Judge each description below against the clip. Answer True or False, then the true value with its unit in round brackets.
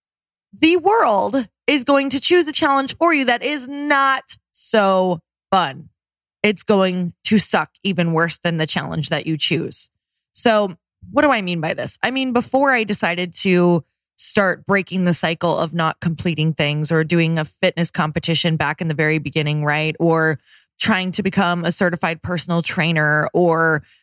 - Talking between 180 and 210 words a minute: False (170 wpm)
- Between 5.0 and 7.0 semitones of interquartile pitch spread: True (5.3 semitones)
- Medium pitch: True (175 Hz)